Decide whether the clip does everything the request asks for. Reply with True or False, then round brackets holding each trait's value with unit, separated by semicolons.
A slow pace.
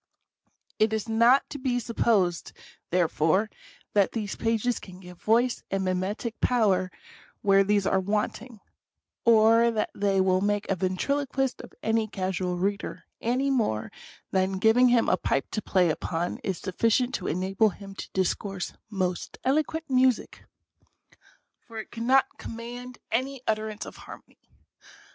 False (150 wpm)